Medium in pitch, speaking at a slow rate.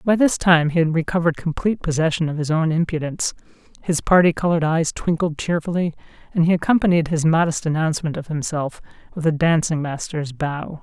No: medium, 160 Hz; average, 170 wpm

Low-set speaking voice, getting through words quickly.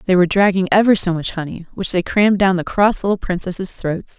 No: medium, 185 Hz; fast, 230 wpm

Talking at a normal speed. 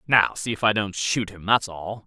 No: fast, 260 wpm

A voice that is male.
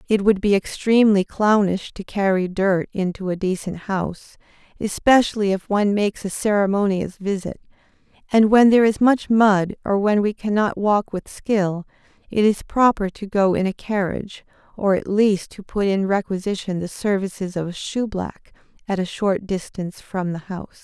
No: female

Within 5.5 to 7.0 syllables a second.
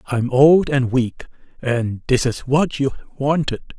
No: 3.8 syllables/s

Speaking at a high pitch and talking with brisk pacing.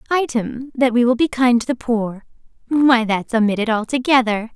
No: high, 240 Hz; average, 170 wpm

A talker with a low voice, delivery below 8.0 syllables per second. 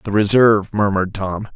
Yes: low, 100 Hz; 5.8 syllables/s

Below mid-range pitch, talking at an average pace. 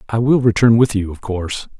No: low, 110 Hz; fast, 235 wpm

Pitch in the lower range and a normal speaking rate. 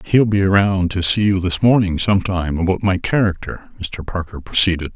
Yes: very low, 95 Hz; average, 180 wpm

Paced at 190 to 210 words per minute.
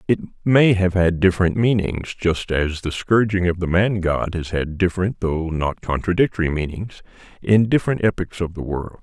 No: average, 180 wpm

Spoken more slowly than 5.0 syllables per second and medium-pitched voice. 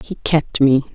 Yes: 4.0 syllables/s; medium, 145 Hz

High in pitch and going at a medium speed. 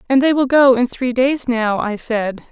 No: very high, 250 Hz; fast, 240 wpm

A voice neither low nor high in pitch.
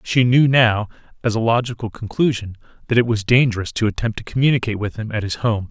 No: low, 115 Hz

